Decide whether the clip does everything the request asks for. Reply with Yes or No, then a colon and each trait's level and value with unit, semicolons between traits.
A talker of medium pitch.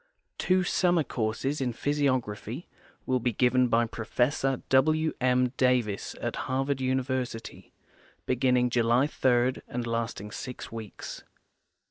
No: low, 125 Hz